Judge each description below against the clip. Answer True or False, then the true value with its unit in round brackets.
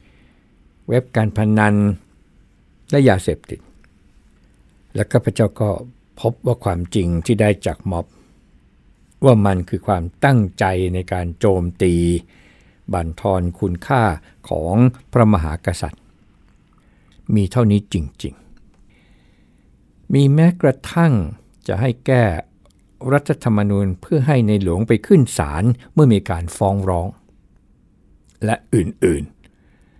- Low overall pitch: True (100 Hz)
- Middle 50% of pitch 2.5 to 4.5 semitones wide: False (5.3 semitones)